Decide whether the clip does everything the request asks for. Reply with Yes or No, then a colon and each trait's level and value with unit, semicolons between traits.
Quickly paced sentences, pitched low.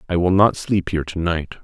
Yes: fast, 220 wpm; very low, 85 Hz